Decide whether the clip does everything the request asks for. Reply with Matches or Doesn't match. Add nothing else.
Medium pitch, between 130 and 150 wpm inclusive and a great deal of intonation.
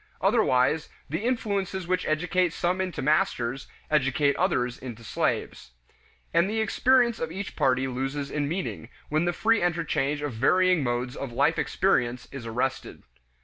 Matches